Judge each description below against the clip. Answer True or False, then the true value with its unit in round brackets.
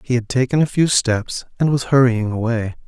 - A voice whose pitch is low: True (125 Hz)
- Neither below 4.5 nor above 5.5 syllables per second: True (5.1 syllables/s)